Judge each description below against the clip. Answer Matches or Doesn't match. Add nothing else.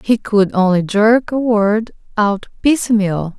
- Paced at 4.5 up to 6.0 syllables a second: Doesn't match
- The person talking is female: Matches